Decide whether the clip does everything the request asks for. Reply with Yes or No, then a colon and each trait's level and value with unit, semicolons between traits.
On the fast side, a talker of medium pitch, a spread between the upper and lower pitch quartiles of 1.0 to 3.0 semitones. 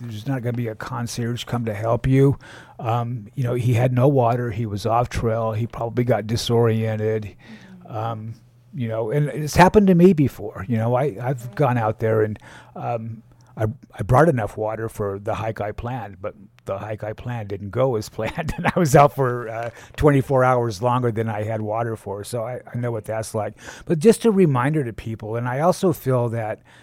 No: fast, 210 wpm; low, 115 Hz; narrow, 2.5 semitones